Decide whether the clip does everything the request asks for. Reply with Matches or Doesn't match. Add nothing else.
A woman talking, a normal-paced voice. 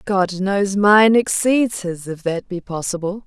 Matches